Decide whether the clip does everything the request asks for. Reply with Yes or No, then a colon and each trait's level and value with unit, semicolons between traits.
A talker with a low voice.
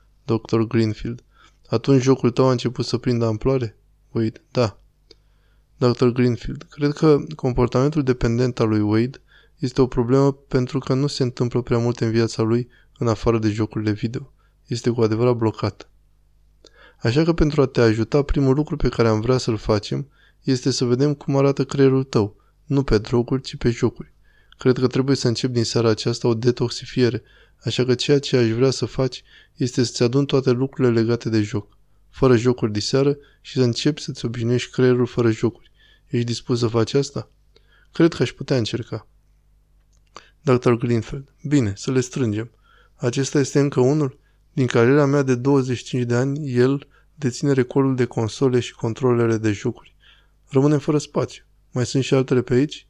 Yes: low, 125 Hz